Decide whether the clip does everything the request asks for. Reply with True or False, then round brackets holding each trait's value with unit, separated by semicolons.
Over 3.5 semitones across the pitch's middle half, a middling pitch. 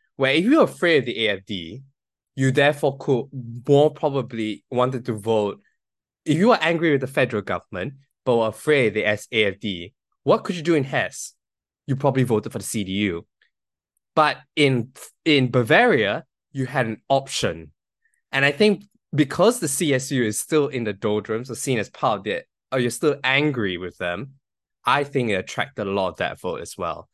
False (5.0 semitones; 130 Hz)